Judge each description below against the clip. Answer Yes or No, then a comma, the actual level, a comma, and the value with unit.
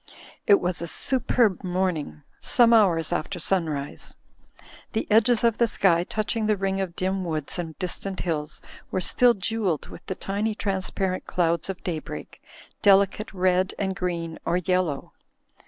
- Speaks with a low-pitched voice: No, medium, 185 Hz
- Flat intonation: No, average, 3.3 semitones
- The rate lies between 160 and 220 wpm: No, average, 150 wpm